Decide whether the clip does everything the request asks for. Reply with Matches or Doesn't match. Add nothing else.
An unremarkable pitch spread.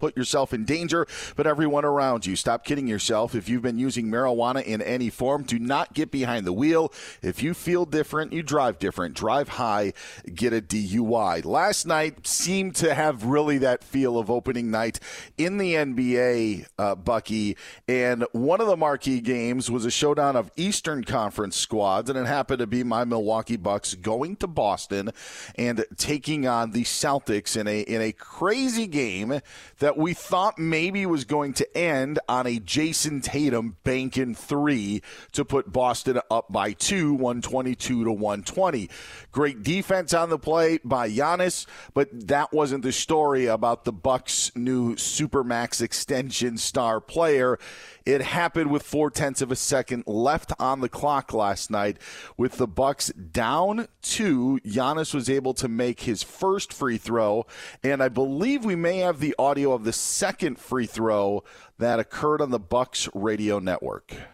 Matches